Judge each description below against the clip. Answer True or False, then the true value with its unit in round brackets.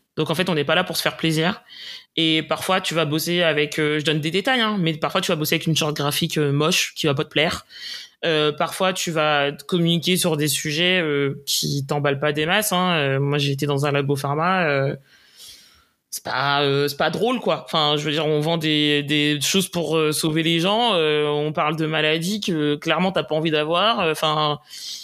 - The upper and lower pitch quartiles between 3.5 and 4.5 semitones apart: False (2.5 semitones)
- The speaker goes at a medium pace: False (230 wpm)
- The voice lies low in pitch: False (155 Hz)